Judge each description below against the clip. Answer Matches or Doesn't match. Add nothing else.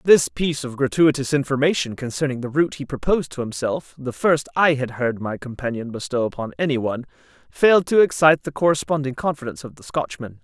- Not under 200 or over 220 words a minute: Doesn't match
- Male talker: Matches